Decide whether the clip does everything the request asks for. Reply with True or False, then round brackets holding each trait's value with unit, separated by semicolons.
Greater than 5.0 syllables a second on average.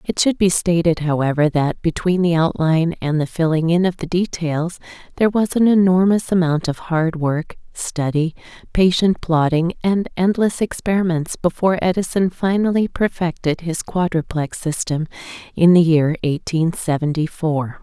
False (4.7 syllables/s)